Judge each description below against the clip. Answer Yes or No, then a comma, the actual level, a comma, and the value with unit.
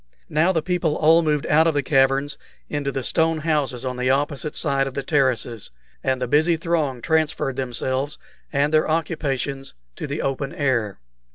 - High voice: No, medium, 145 Hz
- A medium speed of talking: Yes, average, 175 wpm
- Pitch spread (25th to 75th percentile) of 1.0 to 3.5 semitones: Yes, average, 2.8 semitones